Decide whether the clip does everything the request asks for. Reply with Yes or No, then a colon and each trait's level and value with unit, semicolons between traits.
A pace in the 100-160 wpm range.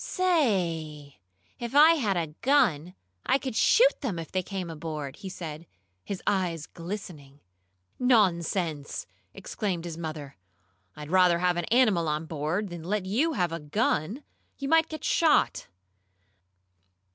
Yes: average, 140 wpm